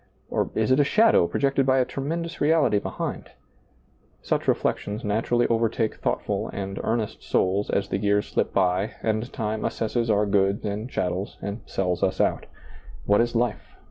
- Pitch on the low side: Yes, low, 110 Hz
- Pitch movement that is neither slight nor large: Yes, average, 3.4 semitones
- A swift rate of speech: No, average, 165 wpm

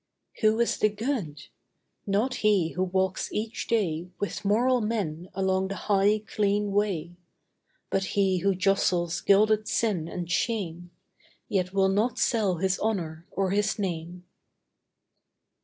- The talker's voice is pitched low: No, high, 195 Hz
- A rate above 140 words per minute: No, slow, 135 wpm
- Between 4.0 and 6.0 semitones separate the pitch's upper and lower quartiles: No, average, 2.9 semitones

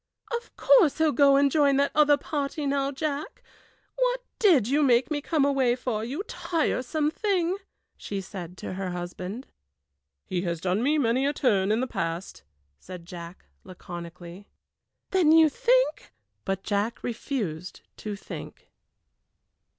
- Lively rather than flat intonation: Yes, wide, 8.0 semitones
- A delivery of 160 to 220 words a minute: No, average, 150 wpm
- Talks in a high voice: Yes, very high, 260 Hz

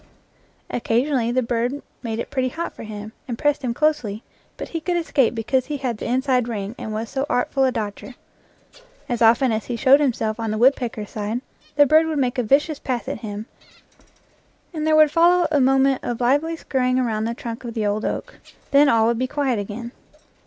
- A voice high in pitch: Yes, very high, 250 Hz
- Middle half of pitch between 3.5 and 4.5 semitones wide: Yes, average, 3.8 semitones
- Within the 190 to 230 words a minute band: Yes, fast, 205 wpm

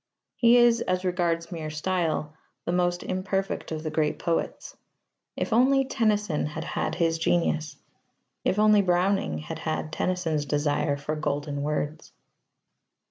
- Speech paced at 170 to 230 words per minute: No, slow, 135 wpm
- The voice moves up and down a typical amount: Yes, average, 3.8 semitones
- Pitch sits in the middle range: Yes, medium, 165 Hz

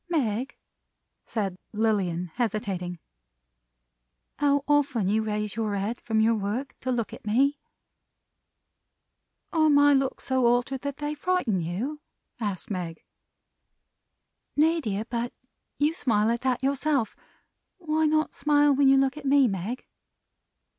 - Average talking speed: No, slow, 130 wpm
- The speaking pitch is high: Yes, high, 245 Hz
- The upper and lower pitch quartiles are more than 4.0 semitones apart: Yes, average, 5.3 semitones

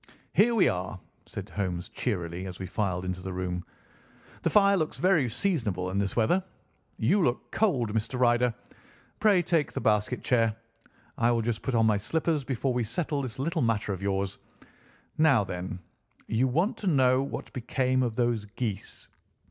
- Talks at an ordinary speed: Yes, average, 170 wpm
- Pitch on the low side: Yes, low, 120 Hz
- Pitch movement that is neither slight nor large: No, wide, 5.7 semitones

